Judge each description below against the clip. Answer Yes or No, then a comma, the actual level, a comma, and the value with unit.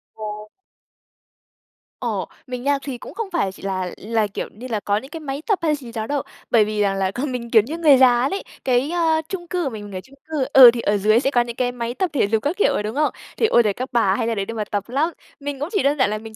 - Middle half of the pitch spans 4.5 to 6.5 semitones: Yes, average, 5.1 semitones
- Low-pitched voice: No, high, 245 Hz